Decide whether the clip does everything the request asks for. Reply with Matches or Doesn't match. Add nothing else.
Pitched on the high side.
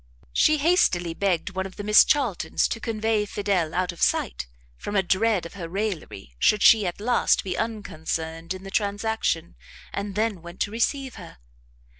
Matches